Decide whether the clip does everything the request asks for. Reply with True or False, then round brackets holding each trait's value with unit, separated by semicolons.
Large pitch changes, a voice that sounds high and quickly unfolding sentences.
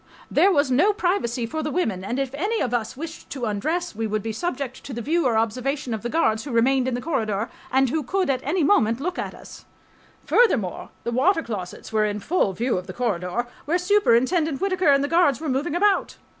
True (6.5 semitones; 265 Hz; 225 wpm)